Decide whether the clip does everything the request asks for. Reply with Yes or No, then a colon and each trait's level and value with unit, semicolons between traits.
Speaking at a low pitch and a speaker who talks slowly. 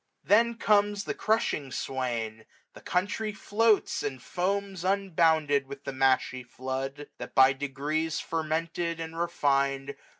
No: medium, 160 Hz; slow, 125 wpm